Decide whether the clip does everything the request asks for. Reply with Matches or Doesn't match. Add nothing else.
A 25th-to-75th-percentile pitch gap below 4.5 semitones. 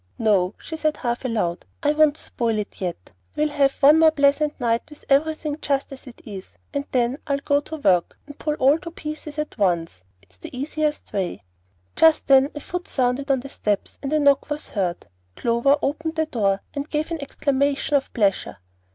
Doesn't match